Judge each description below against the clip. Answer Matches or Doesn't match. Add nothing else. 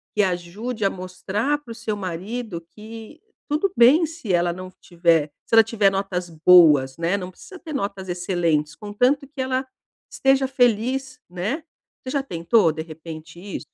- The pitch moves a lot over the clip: Matches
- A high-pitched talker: Matches